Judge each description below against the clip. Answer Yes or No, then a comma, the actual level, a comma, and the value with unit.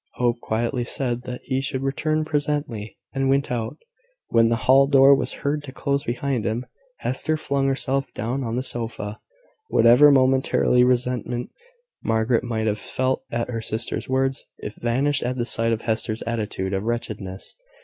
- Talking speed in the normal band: Yes, average, 165 wpm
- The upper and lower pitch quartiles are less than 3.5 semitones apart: Yes, average, 2.9 semitones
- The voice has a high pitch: No, low, 125 Hz